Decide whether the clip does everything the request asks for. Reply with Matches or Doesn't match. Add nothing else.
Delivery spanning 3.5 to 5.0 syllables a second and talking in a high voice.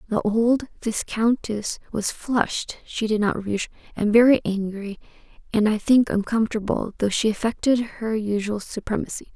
Matches